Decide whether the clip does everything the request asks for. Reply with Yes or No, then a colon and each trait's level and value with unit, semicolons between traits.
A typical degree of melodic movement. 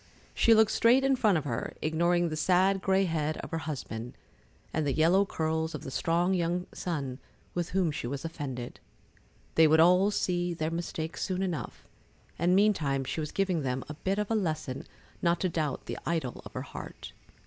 Yes: average, 3.4 semitones